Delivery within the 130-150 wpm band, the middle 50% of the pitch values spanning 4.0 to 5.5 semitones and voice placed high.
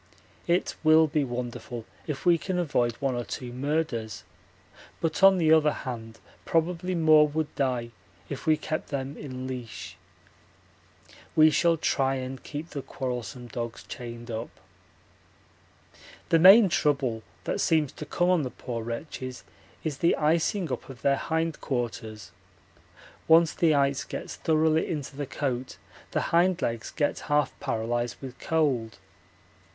No: average, 145 wpm; average, 4.7 semitones; medium, 140 Hz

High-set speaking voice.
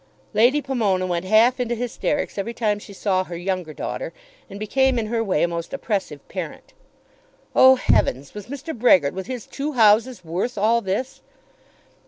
Yes: high, 215 Hz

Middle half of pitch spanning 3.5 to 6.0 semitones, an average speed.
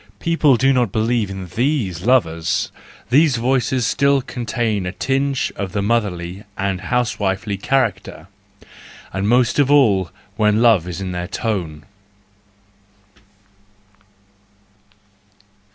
No: average, 5.0 semitones; slow, 110 wpm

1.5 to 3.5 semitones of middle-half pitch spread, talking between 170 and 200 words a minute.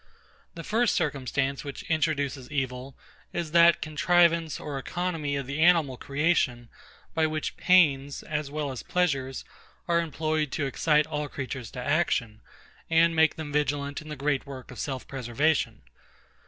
No: average, 3.0 semitones; average, 150 wpm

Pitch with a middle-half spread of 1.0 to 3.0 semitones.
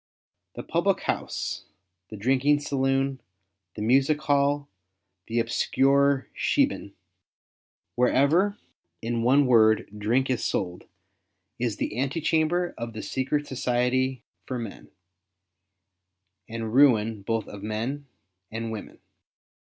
No: average, 3.7 semitones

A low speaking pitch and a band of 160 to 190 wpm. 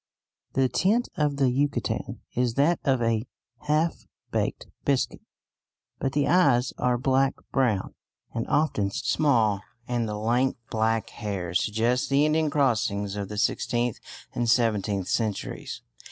No: low, 120 Hz; slow, 135 wpm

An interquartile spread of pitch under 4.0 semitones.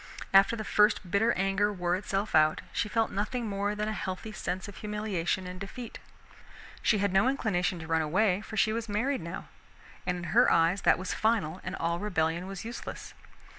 Yes: average, 3.2 semitones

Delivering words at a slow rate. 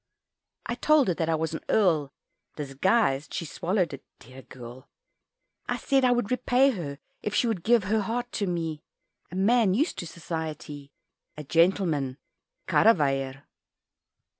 No: average, 150 wpm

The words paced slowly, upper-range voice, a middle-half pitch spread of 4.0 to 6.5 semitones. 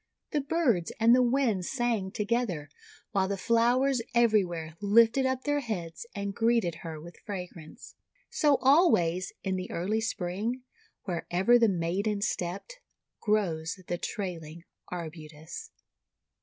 Yes: slow, 125 wpm; high, 200 Hz; wide, 5.5 semitones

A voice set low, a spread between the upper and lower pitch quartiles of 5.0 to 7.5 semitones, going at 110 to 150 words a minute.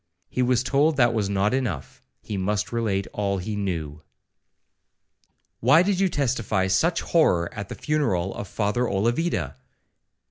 Yes: low, 105 Hz; wide, 5.4 semitones; average, 145 wpm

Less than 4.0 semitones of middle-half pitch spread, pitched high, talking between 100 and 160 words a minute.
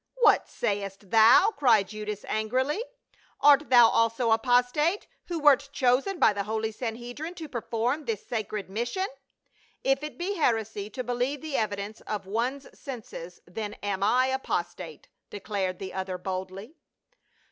No: average, 4.8 semitones; high, 230 Hz; average, 150 wpm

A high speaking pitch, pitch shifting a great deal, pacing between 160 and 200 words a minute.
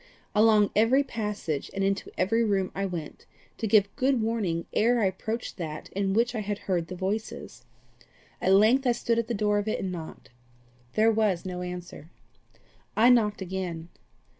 No: high, 205 Hz; average, 3.4 semitones; average, 175 wpm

